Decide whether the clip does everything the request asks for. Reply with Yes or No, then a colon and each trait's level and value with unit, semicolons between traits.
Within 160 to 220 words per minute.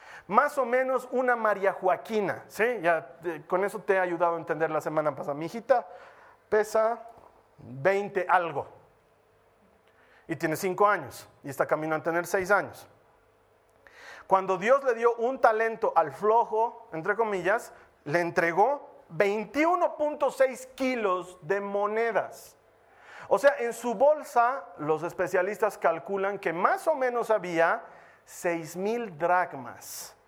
No: average, 130 wpm